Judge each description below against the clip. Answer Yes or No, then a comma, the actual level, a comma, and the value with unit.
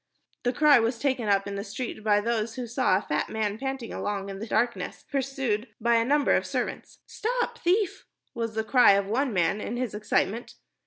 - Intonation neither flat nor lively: Yes, average, 4.0 semitones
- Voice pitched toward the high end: Yes, high, 230 Hz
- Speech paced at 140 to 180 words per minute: No, fast, 205 wpm